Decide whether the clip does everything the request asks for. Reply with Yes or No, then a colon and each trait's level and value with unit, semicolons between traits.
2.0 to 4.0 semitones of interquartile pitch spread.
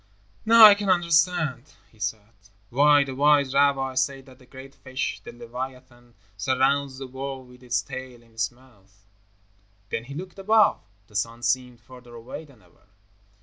Yes: average, 2.8 semitones